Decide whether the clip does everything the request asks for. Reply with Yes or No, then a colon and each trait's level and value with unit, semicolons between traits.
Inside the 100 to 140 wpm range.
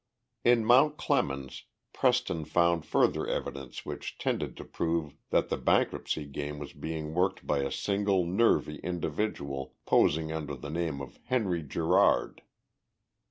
Yes: slow, 135 wpm